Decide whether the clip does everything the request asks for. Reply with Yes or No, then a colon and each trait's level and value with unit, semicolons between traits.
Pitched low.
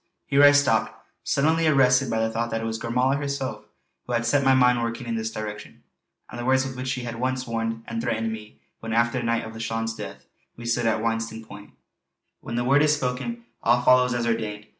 Yes: low, 120 Hz